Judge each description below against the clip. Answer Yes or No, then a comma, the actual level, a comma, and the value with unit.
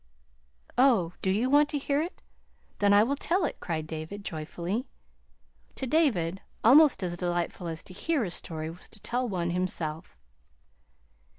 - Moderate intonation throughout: No, wide, 7.5 semitones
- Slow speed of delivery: No, average, 160 wpm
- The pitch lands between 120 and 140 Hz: No, high, 195 Hz